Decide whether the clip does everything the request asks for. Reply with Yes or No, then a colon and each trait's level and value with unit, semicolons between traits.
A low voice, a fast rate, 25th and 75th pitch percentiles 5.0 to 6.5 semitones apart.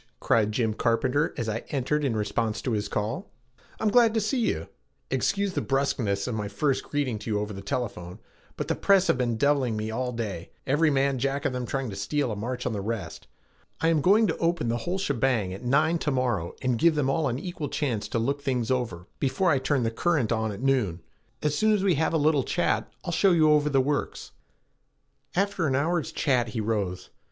Yes: low, 130 Hz; fast, 225 wpm; wide, 5.4 semitones